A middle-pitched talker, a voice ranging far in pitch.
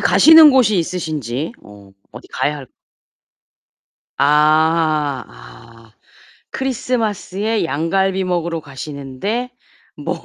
Yes: medium, 160 Hz; wide, 6.3 semitones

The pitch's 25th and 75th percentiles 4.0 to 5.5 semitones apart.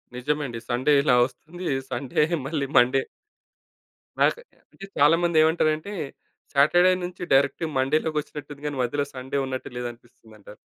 No: average, 3.5 semitones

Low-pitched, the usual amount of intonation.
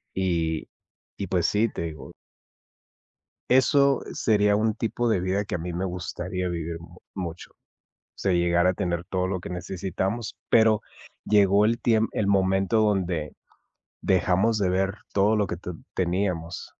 Yes: very low, 95 Hz; average, 3.0 semitones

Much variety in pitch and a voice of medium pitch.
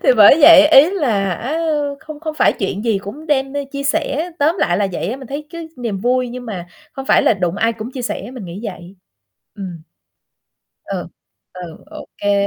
No: wide, 6.3 semitones; high, 245 Hz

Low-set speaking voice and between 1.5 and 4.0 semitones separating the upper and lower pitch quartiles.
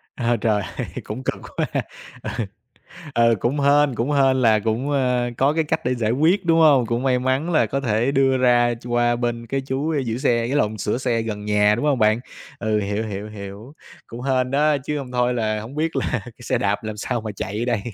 Yes: low, 120 Hz; average, 3.6 semitones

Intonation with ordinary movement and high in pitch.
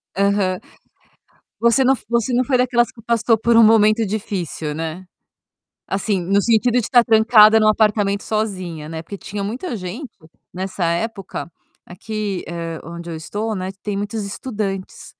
Yes: average, 3.5 semitones; high, 210 Hz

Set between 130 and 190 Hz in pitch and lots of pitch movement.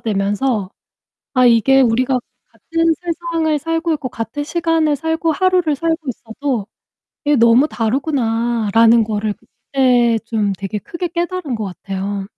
No: very high, 255 Hz; wide, 6.3 semitones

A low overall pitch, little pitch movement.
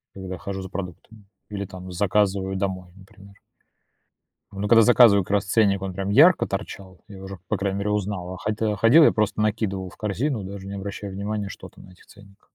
Yes: low, 100 Hz; narrow, 1.6 semitones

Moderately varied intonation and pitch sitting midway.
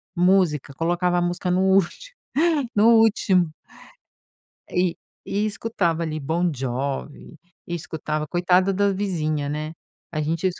Yes: average, 3.5 semitones; medium, 175 Hz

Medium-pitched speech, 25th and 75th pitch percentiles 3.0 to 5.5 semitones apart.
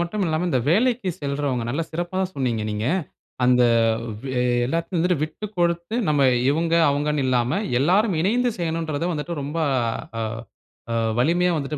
Yes: medium, 160 Hz; average, 3.9 semitones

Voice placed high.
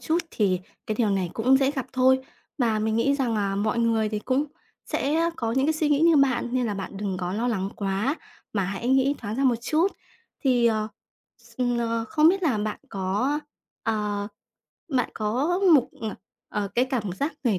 Yes: high, 230 Hz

